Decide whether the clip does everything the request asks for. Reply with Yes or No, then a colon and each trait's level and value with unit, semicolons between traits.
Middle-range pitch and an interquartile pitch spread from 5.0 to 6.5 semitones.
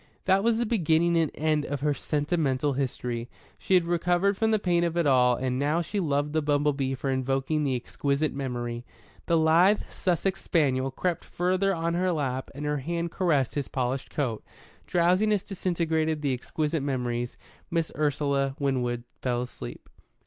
No: medium, 150 Hz; average, 4.4 semitones